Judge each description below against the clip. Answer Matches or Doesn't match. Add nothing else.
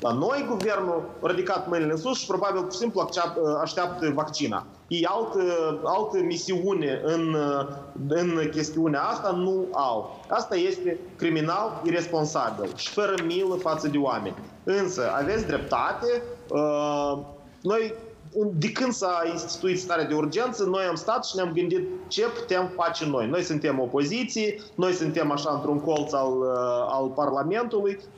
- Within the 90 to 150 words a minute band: Matches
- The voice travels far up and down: Doesn't match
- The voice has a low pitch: Doesn't match